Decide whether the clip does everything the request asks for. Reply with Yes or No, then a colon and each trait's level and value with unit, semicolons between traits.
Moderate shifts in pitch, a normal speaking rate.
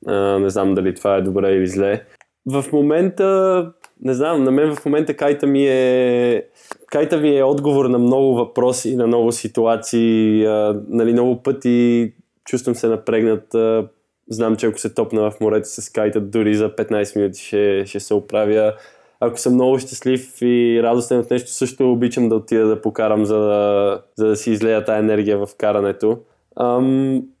No: average, 3.4 semitones; fast, 175 wpm